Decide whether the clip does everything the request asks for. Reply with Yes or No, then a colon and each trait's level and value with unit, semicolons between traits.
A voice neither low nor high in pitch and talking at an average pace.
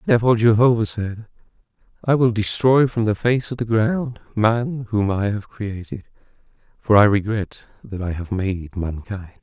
No: low, 110 Hz; average, 160 wpm